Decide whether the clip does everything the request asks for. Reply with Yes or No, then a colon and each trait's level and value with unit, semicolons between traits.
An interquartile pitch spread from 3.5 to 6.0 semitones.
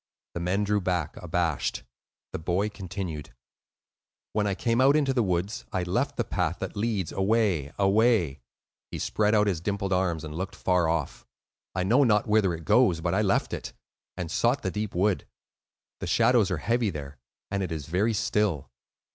Yes: average, 3.8 semitones